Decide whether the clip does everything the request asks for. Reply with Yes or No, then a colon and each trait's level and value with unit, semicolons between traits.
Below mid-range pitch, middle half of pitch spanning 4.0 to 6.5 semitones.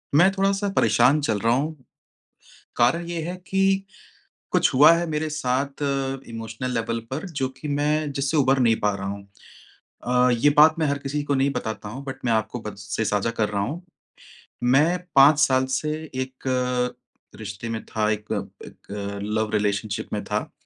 Yes: low, 130 Hz; average, 5.1 semitones